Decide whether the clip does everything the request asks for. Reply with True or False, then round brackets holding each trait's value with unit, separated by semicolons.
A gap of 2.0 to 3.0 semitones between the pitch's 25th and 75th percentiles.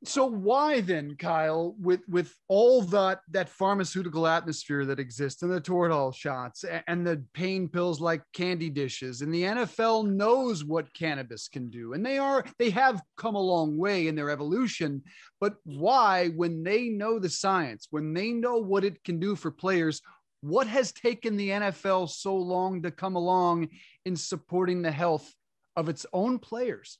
False (4.1 semitones)